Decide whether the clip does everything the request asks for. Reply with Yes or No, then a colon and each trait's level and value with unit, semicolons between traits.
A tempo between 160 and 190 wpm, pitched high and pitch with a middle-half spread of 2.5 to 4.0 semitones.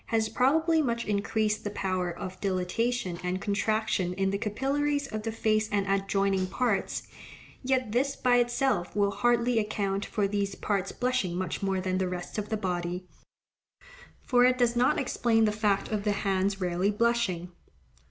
Yes: average, 165 wpm; high, 210 Hz; average, 3.7 semitones